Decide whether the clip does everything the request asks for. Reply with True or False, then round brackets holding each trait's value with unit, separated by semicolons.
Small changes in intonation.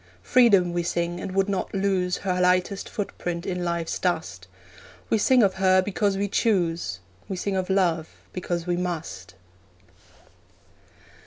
True (2.2 semitones)